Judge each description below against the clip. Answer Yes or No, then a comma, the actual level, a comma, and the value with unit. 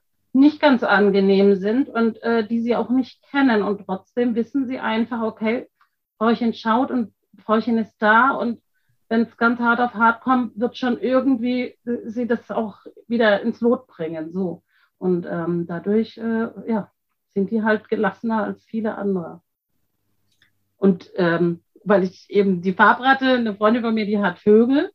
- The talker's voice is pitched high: Yes, high, 225 Hz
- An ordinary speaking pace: Yes, average, 165 wpm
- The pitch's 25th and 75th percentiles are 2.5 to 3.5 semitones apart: Yes, average, 3.2 semitones